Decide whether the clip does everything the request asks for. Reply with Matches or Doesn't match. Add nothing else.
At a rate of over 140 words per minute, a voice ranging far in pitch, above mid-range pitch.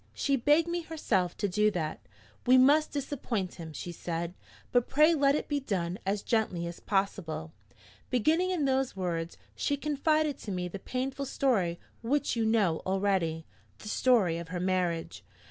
Matches